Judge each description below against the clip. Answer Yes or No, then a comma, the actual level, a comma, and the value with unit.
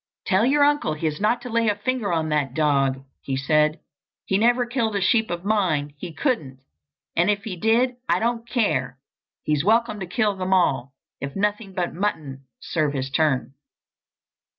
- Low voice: No, medium, 185 Hz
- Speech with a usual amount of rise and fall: No, wide, 7.0 semitones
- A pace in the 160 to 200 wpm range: Yes, average, 175 wpm